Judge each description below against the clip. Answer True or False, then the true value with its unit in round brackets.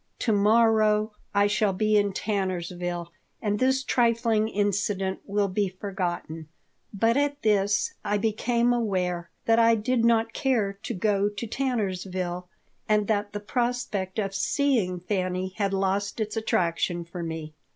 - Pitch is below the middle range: False (205 Hz)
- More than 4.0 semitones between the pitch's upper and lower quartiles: False (3.1 semitones)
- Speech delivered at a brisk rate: False (140 wpm)